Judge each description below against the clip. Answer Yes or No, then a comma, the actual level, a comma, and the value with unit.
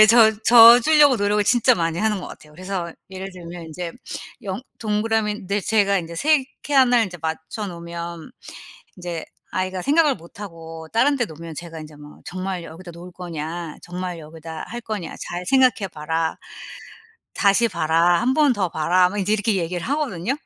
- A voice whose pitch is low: No, medium, 185 Hz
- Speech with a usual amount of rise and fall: Yes, average, 4.6 semitones